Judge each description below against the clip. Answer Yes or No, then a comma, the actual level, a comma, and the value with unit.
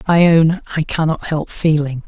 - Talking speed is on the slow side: No, average, 200 wpm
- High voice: No, medium, 160 Hz